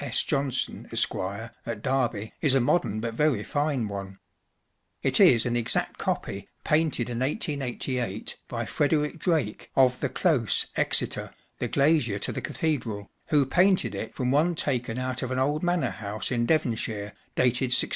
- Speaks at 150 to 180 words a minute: Yes, average, 160 wpm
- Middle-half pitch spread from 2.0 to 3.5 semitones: No, average, 4.5 semitones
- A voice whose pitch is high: No, low, 125 Hz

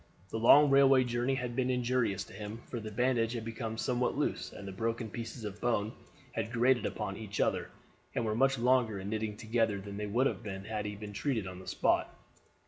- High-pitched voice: No, low, 115 Hz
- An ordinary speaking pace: No, fast, 220 wpm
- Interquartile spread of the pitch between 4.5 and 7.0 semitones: No, average, 2.8 semitones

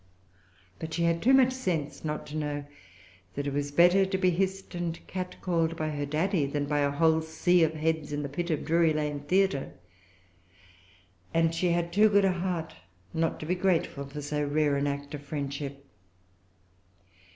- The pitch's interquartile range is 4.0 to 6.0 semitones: No, average, 3.4 semitones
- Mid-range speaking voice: Yes, medium, 160 Hz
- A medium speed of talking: Yes, average, 185 wpm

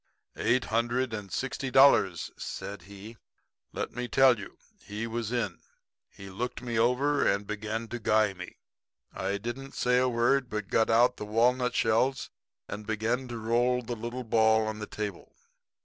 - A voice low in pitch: Yes, low, 115 Hz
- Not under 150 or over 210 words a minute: Yes, average, 165 wpm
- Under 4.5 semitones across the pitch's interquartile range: Yes, average, 2.7 semitones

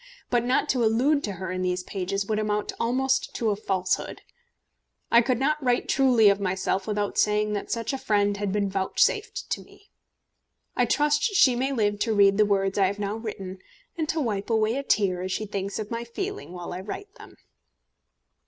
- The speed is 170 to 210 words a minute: Yes, average, 200 wpm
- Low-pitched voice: No, high, 210 Hz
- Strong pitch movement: No, average, 4.1 semitones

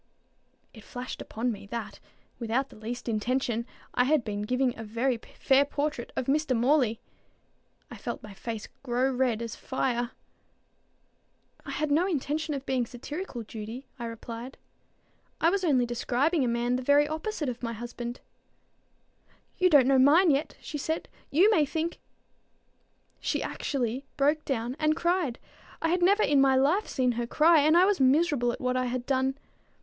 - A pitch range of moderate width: Yes, average, 4.1 semitones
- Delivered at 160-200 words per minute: Yes, average, 170 wpm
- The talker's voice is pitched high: Yes, very high, 260 Hz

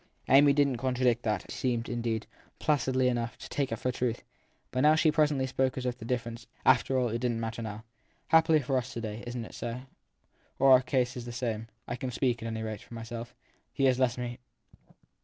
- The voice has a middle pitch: No, low, 125 Hz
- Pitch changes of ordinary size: No, narrow, 2.0 semitones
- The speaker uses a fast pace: Yes, fast, 215 wpm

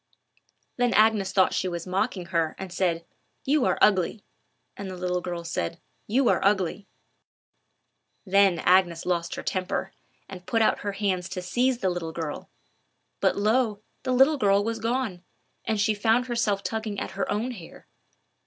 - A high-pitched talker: Yes, high, 200 Hz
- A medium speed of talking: Yes, average, 165 wpm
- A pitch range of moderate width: Yes, average, 3.7 semitones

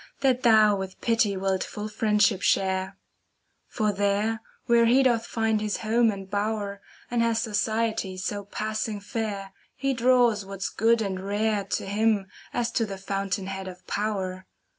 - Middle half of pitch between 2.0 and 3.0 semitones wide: Yes, narrow, 2.4 semitones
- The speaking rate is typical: Yes, average, 160 wpm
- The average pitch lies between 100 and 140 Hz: No, high, 210 Hz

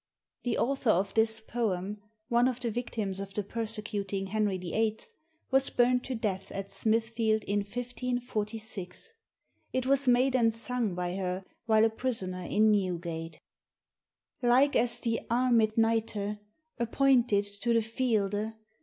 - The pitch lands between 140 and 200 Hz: No, high, 220 Hz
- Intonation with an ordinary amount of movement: Yes, average, 3.2 semitones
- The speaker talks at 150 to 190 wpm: No, average, 140 wpm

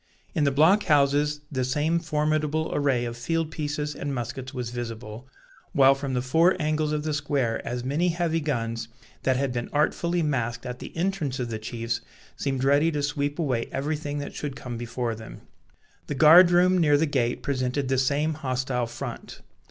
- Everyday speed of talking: Yes, average, 185 wpm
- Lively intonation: No, average, 3.6 semitones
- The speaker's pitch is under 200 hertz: Yes, medium, 140 Hz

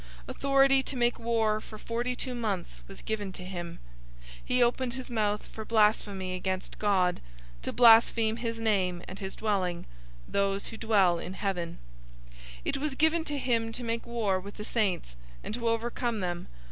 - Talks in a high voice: Yes, high, 220 Hz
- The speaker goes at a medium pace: Yes, average, 175 wpm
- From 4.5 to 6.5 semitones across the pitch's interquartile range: No, average, 3.8 semitones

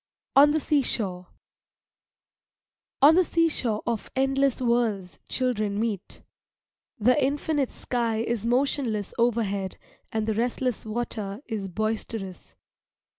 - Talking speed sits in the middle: No, slow, 105 wpm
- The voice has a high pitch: Yes, high, 230 Hz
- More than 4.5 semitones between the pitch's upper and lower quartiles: No, average, 3.9 semitones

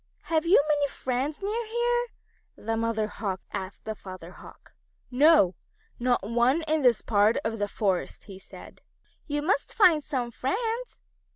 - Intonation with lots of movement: Yes, wide, 7.1 semitones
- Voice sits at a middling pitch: No, very high, 255 Hz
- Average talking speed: Yes, average, 155 wpm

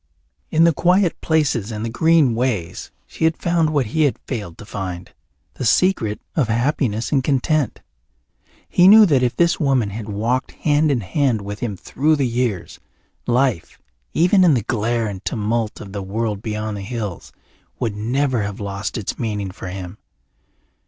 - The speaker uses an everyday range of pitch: No, wide, 5.8 semitones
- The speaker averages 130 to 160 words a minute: No, average, 170 wpm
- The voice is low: Yes, low, 120 Hz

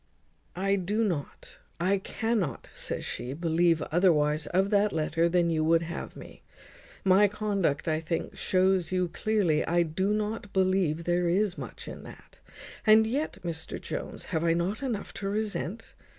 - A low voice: No, medium, 180 Hz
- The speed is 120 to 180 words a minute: Yes, average, 160 wpm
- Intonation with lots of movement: No, average, 3.6 semitones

